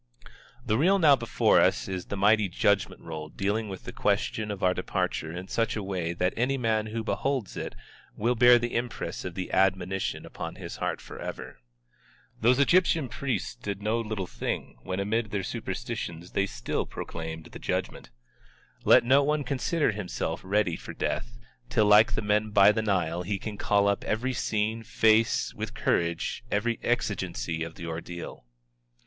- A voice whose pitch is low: Yes, low, 105 Hz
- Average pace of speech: Yes, average, 170 wpm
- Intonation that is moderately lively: Yes, average, 4.0 semitones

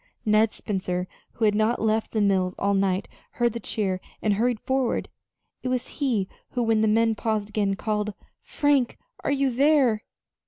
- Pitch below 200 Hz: No, high, 220 Hz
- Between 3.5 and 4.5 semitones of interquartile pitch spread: No, average, 3.0 semitones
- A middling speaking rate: Yes, average, 170 wpm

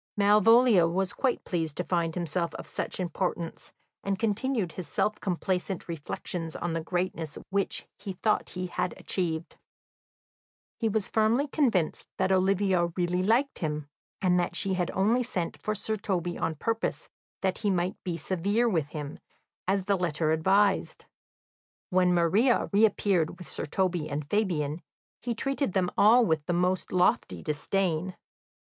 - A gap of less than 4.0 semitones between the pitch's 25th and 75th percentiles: Yes, average, 3.4 semitones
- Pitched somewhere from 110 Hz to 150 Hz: No, medium, 185 Hz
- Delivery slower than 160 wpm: Yes, average, 150 wpm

